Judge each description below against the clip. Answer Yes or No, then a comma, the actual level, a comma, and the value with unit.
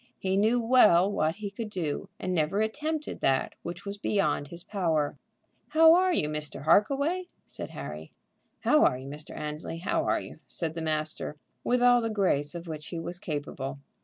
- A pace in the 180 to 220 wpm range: Yes, average, 185 wpm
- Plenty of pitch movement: Yes, wide, 6.3 semitones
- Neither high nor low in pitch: Yes, medium, 175 Hz